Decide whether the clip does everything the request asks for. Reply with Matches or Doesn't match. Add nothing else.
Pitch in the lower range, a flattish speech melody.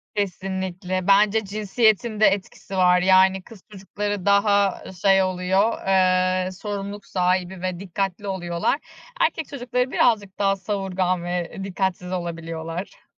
Doesn't match